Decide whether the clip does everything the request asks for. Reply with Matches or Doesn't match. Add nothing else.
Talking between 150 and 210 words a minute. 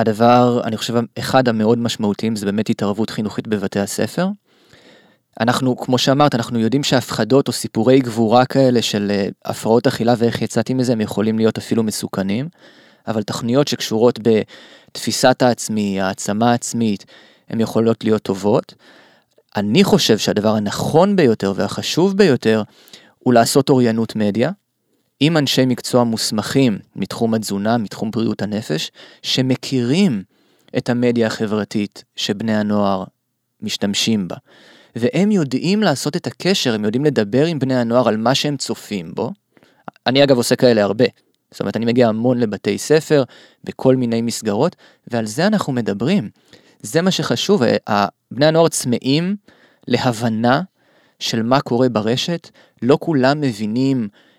Doesn't match